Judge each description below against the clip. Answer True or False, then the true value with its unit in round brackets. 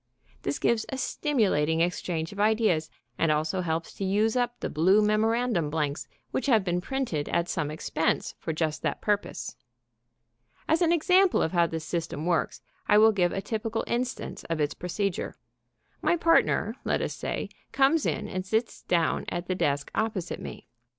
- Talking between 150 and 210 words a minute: True (170 wpm)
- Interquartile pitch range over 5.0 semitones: True (5.5 semitones)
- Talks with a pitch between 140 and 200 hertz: True (190 Hz)